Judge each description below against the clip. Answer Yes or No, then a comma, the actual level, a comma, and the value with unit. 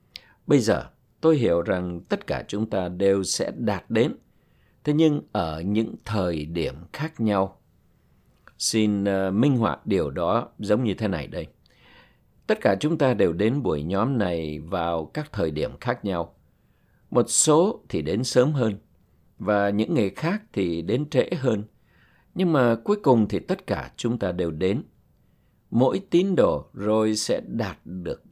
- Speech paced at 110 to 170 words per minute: Yes, slow, 165 wpm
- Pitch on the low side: Yes, low, 105 Hz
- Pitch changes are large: Yes, wide, 6.1 semitones